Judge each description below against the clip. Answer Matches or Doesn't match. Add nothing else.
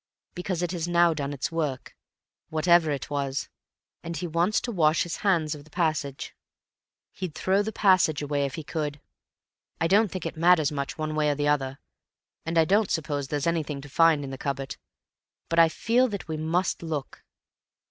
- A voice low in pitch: Doesn't match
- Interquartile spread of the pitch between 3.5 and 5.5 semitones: Doesn't match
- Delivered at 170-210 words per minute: Matches